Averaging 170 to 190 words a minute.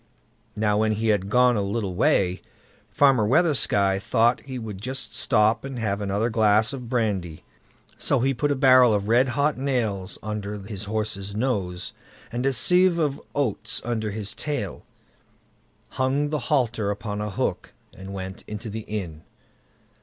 No: average, 160 wpm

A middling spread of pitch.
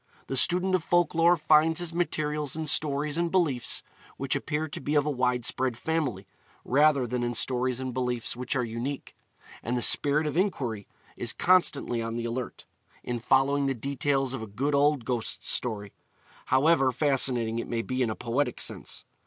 Yes: average, 3.7 semitones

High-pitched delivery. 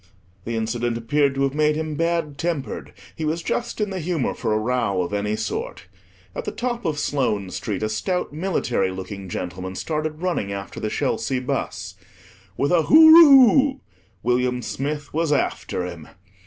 No: medium, 140 Hz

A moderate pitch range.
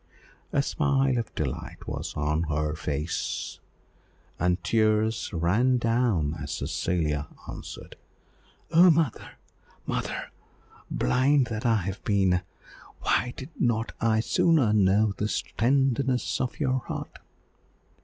No: wide, 6.4 semitones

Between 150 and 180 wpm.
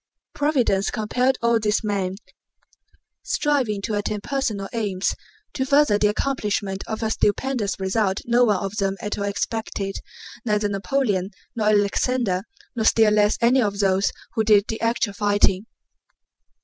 No: average, 140 wpm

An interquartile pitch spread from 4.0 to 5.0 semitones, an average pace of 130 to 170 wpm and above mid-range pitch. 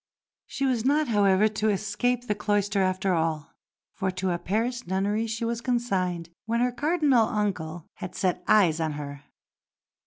Yes: average, 4.4 semitones; average, 160 wpm; high, 205 Hz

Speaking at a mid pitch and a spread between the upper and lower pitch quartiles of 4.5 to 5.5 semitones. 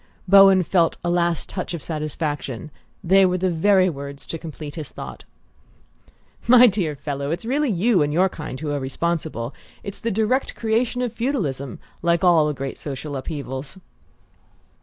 Yes: medium, 170 Hz; average, 5.0 semitones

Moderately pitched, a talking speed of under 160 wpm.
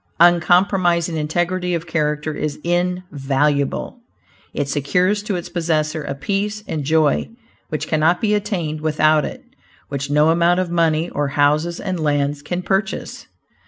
Yes: medium, 160 Hz; average, 140 wpm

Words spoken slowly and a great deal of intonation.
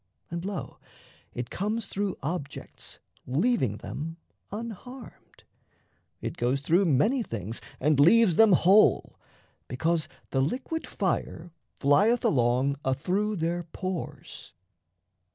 Yes: slow, 105 wpm; wide, 7.1 semitones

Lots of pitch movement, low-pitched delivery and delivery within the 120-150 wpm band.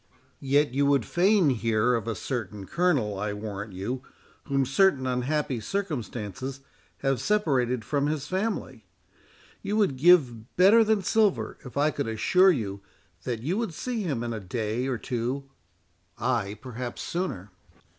Yes: wide, 6.2 semitones; low, 130 Hz; average, 145 wpm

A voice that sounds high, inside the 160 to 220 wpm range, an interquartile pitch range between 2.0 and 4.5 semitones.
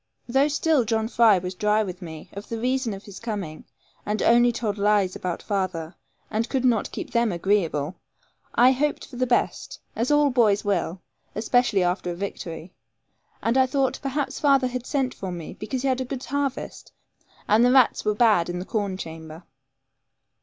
No: high, 220 Hz; average, 185 wpm; average, 5.3 semitones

